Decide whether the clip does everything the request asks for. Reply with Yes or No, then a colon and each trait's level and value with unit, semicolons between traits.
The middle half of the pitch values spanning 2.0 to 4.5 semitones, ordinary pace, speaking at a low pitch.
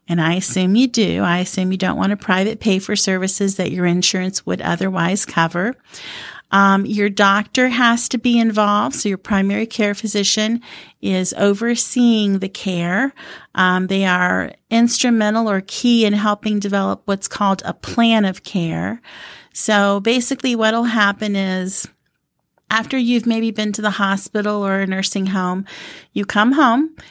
No: average, 2.9 semitones; average, 155 wpm; high, 205 Hz